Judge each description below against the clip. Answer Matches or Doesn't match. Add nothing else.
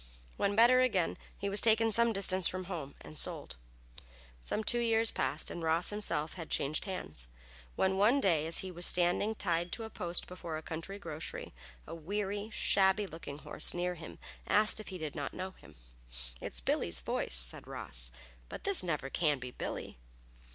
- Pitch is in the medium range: Matches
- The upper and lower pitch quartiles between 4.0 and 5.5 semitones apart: Matches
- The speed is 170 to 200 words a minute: Matches